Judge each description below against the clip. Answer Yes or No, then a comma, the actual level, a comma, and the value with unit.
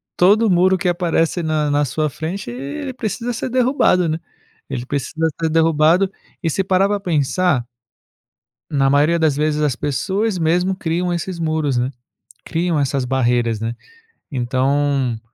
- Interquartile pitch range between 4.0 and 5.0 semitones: Yes, average, 4.6 semitones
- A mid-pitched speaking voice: Yes, medium, 160 Hz